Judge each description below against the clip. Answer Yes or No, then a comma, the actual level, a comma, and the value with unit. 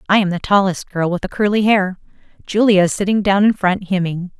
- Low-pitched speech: No, high, 190 Hz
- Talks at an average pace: No, fast, 220 wpm